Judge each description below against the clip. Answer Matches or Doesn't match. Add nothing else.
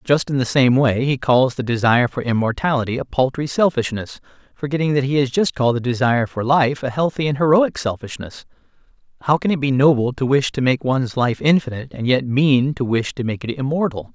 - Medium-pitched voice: Doesn't match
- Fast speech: Matches